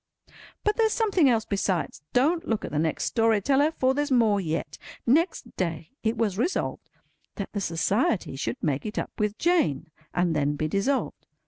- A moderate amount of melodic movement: No, wide, 8.7 semitones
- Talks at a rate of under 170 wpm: No, average, 180 wpm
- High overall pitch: Yes, high, 215 Hz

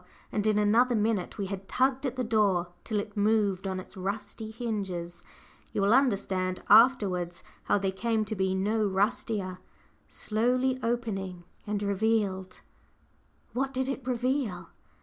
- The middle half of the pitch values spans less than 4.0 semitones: Yes, average, 3.4 semitones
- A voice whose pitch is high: Yes, high, 210 Hz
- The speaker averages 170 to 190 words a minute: No, average, 145 wpm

